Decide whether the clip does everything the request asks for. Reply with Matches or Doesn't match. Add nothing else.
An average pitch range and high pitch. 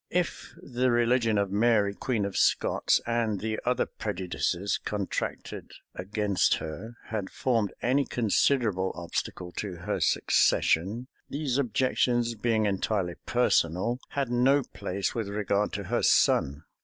Doesn't match